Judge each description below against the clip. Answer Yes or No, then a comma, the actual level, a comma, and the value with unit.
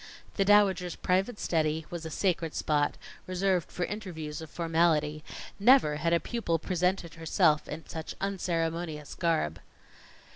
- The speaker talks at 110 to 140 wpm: Yes, slow, 135 wpm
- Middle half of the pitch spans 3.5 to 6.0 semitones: No, average, 2.9 semitones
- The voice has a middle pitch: Yes, medium, 170 Hz